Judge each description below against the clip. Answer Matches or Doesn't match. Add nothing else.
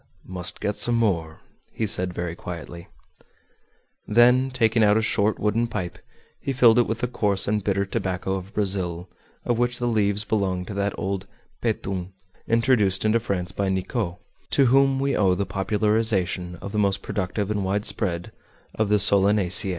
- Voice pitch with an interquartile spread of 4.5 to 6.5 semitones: Doesn't match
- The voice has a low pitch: Matches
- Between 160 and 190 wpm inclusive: Matches